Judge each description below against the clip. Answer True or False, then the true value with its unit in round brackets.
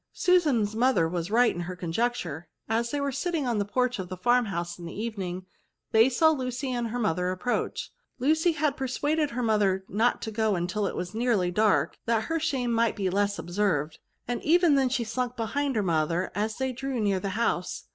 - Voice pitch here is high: True (225 Hz)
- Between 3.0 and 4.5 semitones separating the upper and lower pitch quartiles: False (5.4 semitones)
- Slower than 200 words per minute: False (205 wpm)